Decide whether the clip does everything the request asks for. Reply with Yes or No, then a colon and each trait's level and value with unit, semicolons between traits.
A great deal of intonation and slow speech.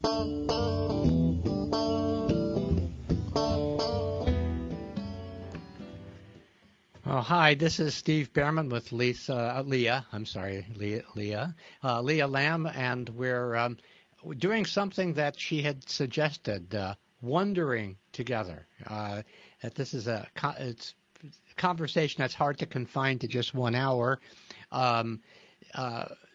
Yes: wide, 6.4 semitones; slow, 110 wpm